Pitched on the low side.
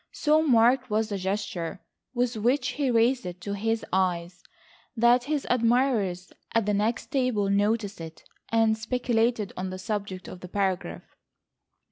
No: high, 220 Hz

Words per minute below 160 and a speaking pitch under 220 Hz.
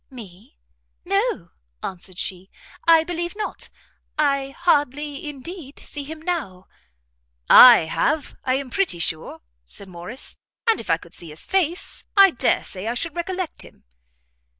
No: average, 145 wpm; very high, 285 Hz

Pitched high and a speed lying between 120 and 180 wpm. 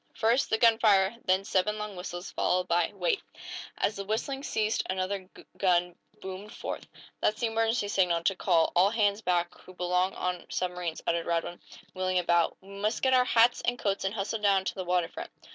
No: high, 195 Hz; average, 190 wpm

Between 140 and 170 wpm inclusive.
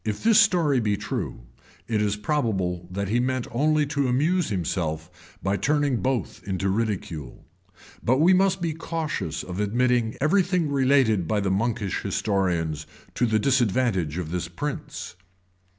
Yes: average, 155 wpm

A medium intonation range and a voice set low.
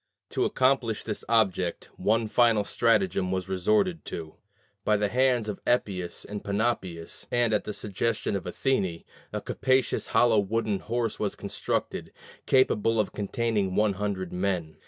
Yes: average, 3.5 semitones; low, 105 Hz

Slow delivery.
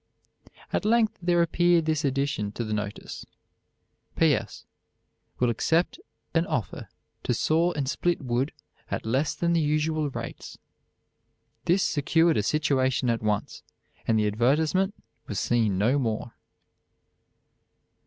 Yes: slow, 130 wpm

